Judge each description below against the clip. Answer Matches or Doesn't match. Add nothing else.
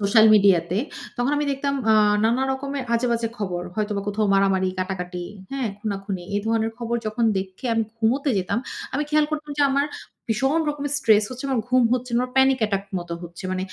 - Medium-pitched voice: Doesn't match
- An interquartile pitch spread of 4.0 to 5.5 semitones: Matches